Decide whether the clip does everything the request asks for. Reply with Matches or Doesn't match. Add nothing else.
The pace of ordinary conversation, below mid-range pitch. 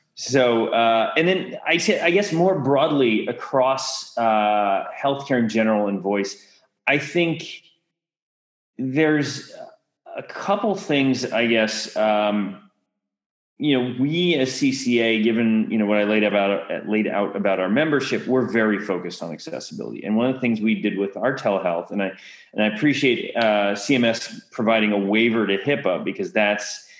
Matches